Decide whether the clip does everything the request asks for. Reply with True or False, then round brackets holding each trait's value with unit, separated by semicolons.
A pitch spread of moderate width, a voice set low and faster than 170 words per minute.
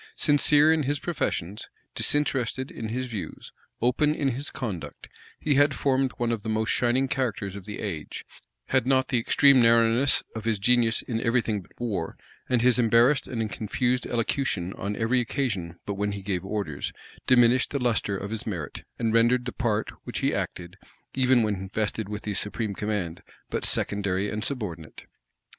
True (3.8 semitones; 115 Hz; 180 wpm)